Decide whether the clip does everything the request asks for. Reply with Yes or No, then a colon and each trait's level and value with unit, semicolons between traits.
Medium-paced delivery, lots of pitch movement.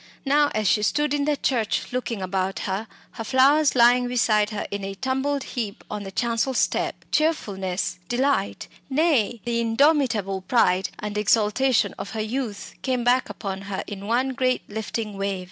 No: average, 165 wpm; average, 4.5 semitones